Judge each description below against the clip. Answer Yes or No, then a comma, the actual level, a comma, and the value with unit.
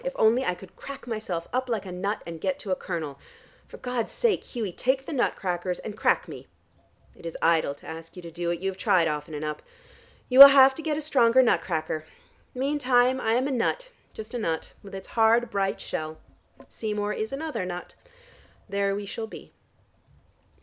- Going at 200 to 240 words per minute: Yes, fast, 205 wpm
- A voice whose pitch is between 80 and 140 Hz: No, high, 210 Hz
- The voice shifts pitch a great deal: Yes, wide, 6.5 semitones